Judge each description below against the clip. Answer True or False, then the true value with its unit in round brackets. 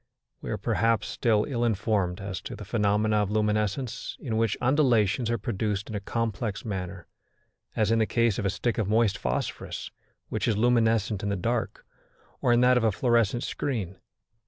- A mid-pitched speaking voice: False (110 Hz)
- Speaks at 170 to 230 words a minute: True (180 wpm)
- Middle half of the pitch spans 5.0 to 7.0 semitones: False (2.5 semitones)